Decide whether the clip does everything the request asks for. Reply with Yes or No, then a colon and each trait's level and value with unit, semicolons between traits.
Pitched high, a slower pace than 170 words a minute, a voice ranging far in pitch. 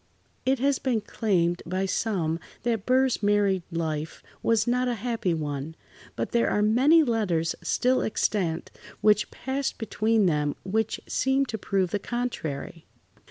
Yes: high, 210 Hz; average, 145 wpm; wide, 6.1 semitones